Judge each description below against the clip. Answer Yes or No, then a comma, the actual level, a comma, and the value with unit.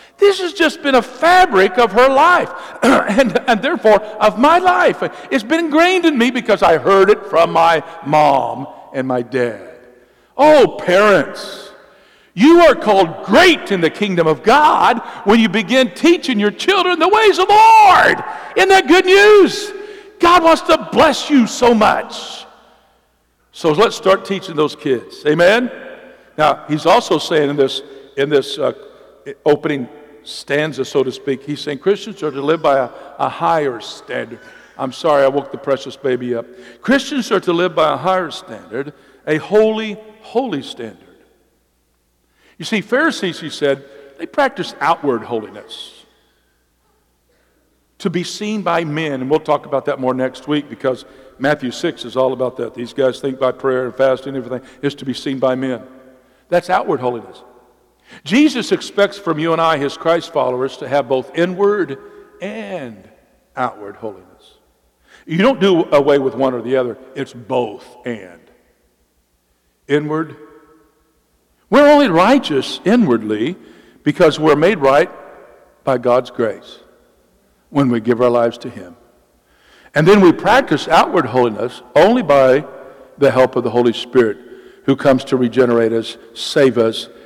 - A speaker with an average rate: Yes, average, 160 wpm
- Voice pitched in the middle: Yes, medium, 155 Hz